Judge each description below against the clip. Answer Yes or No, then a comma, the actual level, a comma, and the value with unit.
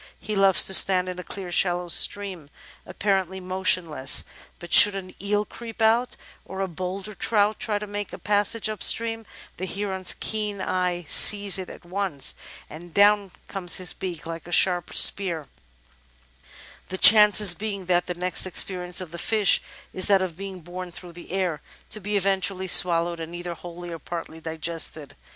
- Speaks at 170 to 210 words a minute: Yes, average, 175 wpm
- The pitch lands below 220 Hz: Yes, medium, 185 Hz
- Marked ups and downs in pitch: No, narrow, 2.5 semitones